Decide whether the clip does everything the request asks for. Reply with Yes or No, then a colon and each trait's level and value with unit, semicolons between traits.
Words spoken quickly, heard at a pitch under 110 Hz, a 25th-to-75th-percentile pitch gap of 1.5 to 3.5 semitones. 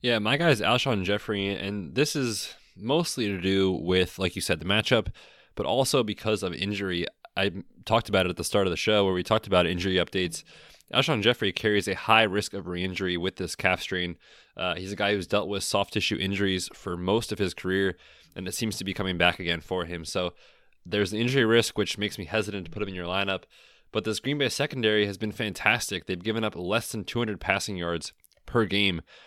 Yes: fast, 230 wpm; low, 100 Hz; average, 2.9 semitones